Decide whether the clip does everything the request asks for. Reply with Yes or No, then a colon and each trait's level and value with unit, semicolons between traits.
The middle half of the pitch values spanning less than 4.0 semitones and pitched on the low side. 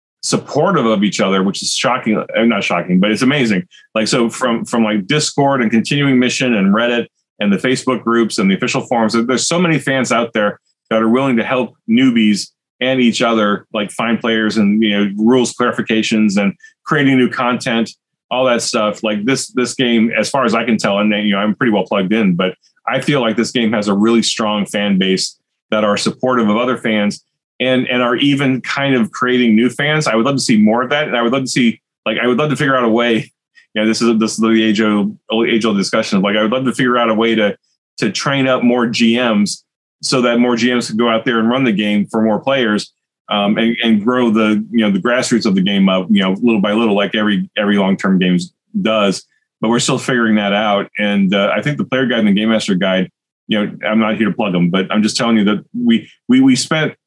Yes: average, 3.3 semitones; low, 115 Hz